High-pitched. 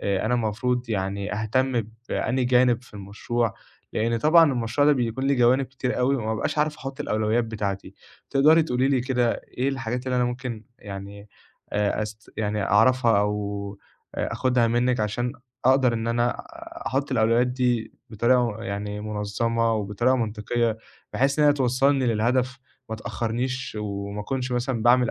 No: low, 120 Hz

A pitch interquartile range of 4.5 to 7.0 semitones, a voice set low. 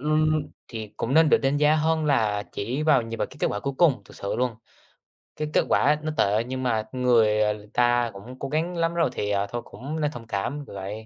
Yes: wide, 5.6 semitones; low, 125 Hz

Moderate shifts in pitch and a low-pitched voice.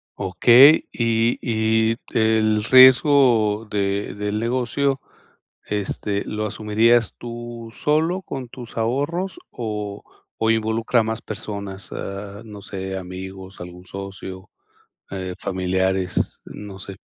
Yes: average, 3.3 semitones; low, 110 Hz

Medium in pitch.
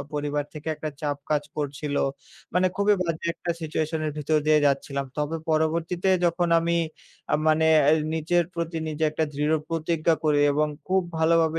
Yes: medium, 155 Hz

